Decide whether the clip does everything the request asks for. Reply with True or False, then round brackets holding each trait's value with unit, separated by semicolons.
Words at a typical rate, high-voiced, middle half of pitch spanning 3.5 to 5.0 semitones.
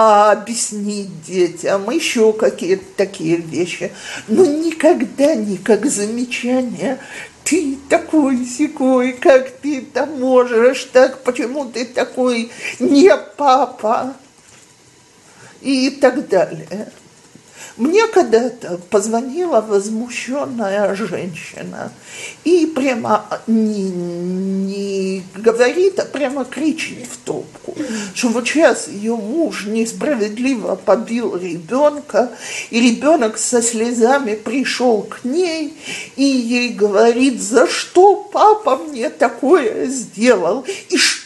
False (95 wpm; 245 Hz; 4.7 semitones)